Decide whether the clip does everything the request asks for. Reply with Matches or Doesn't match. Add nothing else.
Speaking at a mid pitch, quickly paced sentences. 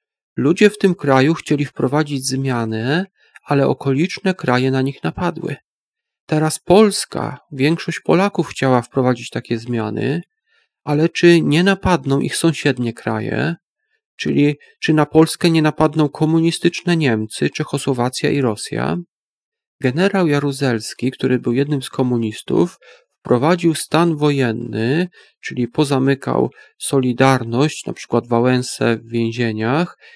Doesn't match